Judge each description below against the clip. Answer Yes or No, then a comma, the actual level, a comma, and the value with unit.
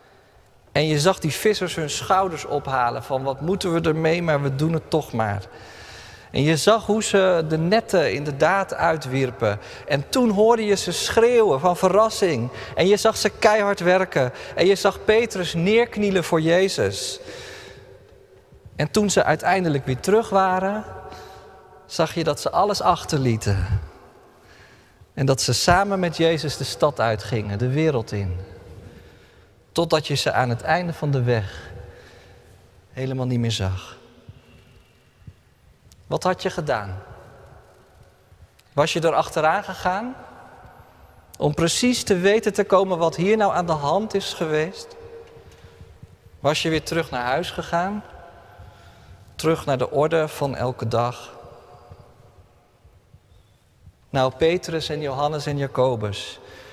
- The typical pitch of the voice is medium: Yes, medium, 155 Hz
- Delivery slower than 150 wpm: Yes, average, 140 wpm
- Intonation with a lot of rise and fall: Yes, wide, 7.9 semitones